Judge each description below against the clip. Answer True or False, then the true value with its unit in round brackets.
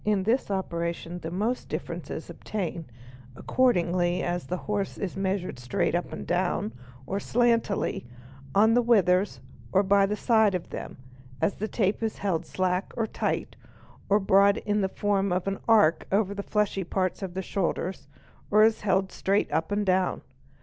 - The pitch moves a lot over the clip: False (2.5 semitones)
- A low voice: False (195 Hz)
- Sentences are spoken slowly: False (175 wpm)